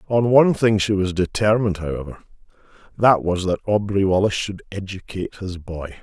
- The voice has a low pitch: Yes, low, 100 Hz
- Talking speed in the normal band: Yes, average, 160 wpm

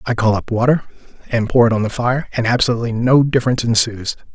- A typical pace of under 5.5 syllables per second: No, 6.7 syllables/s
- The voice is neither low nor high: No, low, 120 Hz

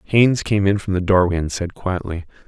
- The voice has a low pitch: Yes, very low, 95 Hz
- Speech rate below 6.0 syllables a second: Yes, 5.5 syllables/s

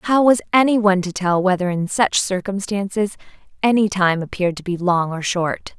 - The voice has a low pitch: No, high, 195 Hz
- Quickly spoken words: No, average, 175 wpm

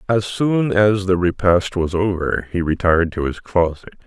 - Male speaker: Yes, male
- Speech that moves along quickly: No, average, 175 wpm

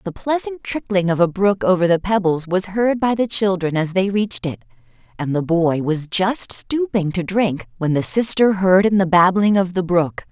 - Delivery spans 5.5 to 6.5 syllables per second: No, 4.8 syllables/s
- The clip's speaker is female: Yes, female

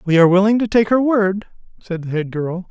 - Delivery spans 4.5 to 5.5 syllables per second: No, 5.7 syllables/s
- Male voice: Yes, male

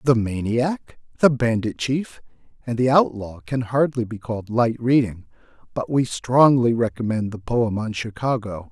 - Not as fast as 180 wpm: Yes, average, 150 wpm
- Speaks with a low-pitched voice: Yes, low, 120 Hz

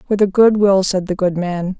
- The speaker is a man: No, female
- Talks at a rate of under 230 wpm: No, fast, 265 wpm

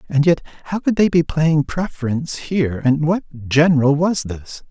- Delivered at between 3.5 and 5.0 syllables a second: Yes, 4.9 syllables/s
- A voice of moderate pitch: Yes, medium, 155 Hz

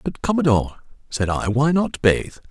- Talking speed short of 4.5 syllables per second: No, 4.9 syllables/s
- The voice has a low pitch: Yes, low, 130 Hz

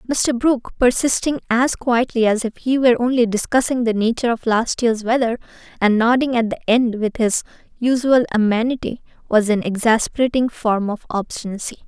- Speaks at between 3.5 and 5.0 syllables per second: No, 5.4 syllables/s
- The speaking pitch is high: Yes, high, 235 Hz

